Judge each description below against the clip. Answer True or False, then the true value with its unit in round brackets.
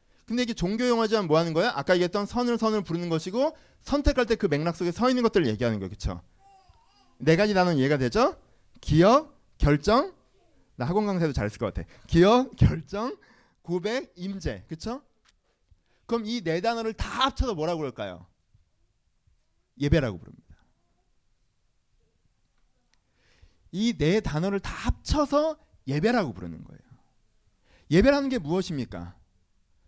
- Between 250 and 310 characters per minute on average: True (295 characters per minute)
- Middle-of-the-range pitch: True (175 Hz)